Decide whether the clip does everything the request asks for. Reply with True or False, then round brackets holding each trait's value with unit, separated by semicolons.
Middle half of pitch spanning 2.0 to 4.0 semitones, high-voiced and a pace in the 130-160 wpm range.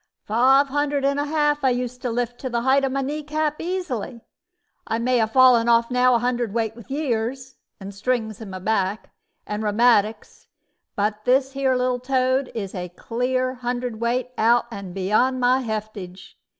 False (3.1 semitones; 245 Hz; 175 wpm)